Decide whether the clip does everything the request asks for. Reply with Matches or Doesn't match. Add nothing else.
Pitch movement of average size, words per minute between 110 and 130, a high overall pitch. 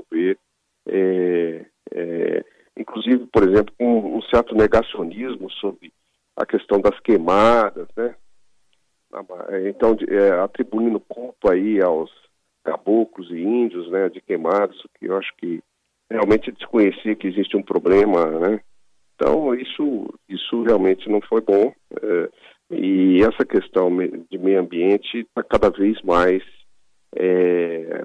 Doesn't match